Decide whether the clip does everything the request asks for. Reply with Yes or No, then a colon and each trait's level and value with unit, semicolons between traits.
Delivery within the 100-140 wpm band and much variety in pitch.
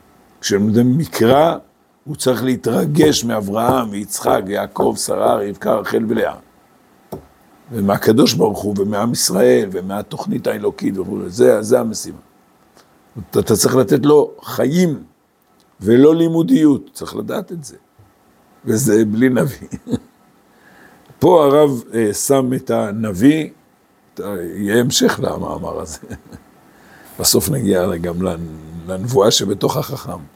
Yes: average, 105 wpm; wide, 6.4 semitones